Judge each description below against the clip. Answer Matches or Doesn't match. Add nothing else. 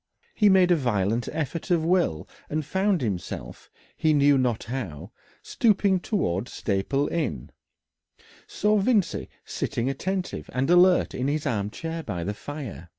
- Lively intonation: Matches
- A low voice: Doesn't match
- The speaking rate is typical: Matches